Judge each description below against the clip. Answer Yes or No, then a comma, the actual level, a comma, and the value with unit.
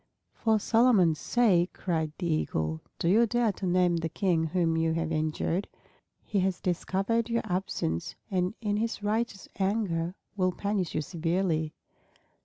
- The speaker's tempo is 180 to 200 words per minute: No, average, 150 wpm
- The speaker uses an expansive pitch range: No, average, 4.0 semitones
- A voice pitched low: No, medium, 185 Hz